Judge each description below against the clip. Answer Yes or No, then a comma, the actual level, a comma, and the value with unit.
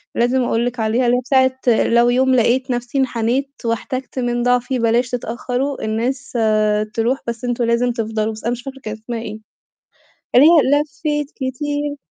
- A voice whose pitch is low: No, high, 245 Hz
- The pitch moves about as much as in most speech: No, narrow, 2.3 semitones